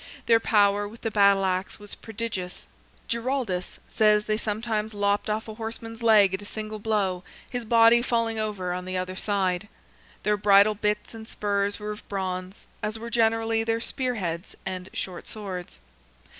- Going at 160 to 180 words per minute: Yes, average, 170 wpm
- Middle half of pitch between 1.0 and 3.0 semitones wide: Yes, narrow, 2.4 semitones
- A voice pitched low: No, high, 210 Hz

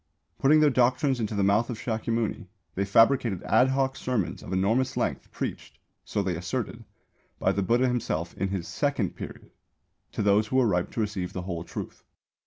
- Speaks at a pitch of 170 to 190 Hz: No, low, 110 Hz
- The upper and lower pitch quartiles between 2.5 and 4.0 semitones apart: No, average, 4.8 semitones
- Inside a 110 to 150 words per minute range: No, average, 185 wpm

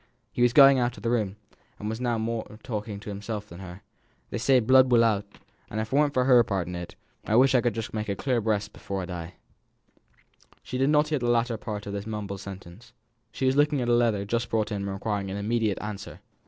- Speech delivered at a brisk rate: Yes, fast, 240 wpm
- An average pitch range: Yes, average, 3.3 semitones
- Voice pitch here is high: No, low, 110 Hz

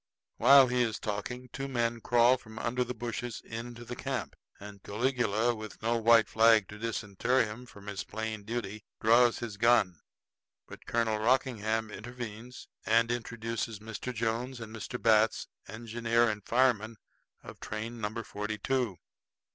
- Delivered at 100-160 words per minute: Yes, average, 150 wpm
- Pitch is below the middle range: Yes, low, 115 Hz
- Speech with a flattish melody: Yes, narrow, 1.9 semitones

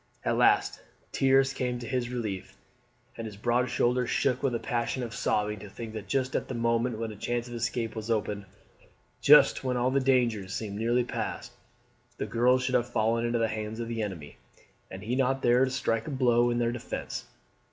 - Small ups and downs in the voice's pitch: Yes, narrow, 2.1 semitones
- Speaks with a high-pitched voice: No, low, 120 Hz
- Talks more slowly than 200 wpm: No, fast, 205 wpm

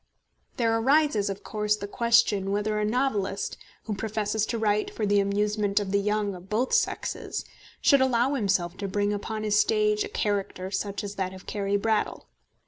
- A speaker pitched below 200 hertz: No, high, 210 Hz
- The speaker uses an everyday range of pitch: No, narrow, 2.2 semitones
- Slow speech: No, average, 180 wpm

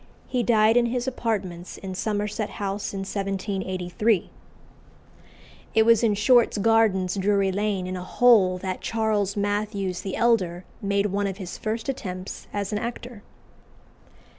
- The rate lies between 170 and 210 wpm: No, average, 140 wpm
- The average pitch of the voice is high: Yes, high, 205 Hz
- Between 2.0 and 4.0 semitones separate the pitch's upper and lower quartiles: Yes, average, 2.8 semitones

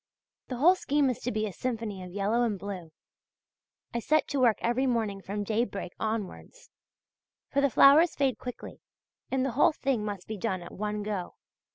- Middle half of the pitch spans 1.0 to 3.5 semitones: No, average, 4.6 semitones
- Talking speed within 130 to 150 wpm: No, average, 185 wpm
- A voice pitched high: Yes, high, 225 Hz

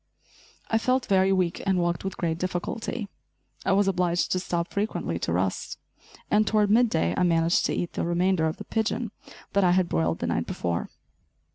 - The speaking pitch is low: No, medium, 185 Hz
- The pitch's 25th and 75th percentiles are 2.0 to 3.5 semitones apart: Yes, average, 3.2 semitones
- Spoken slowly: No, average, 190 wpm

